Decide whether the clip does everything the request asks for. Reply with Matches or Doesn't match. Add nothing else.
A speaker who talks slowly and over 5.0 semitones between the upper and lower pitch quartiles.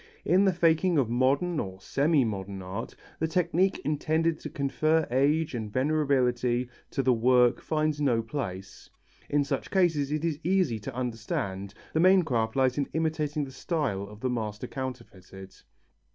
Doesn't match